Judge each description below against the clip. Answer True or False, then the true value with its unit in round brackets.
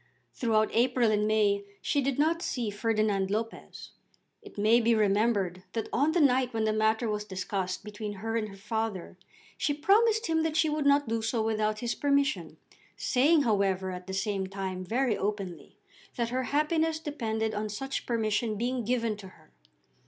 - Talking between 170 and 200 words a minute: True (175 wpm)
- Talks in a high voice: True (220 Hz)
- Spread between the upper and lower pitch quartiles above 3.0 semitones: True (4.0 semitones)